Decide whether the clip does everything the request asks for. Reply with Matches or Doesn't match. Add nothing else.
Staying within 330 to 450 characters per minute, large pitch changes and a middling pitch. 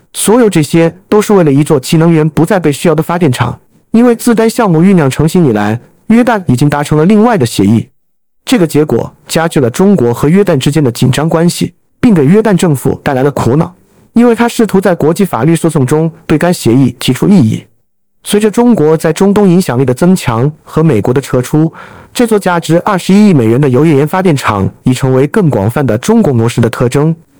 Doesn't match